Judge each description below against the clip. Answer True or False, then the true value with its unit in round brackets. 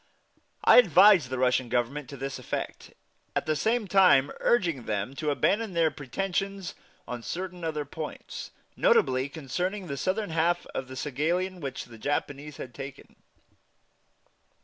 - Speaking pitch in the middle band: True (150 Hz)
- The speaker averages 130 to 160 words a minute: True (140 wpm)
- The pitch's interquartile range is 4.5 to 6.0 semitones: True (5.6 semitones)